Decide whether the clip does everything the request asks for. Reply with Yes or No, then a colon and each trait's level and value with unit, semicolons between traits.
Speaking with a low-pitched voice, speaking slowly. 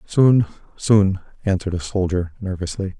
Yes: very low, 95 Hz; slow, 120 wpm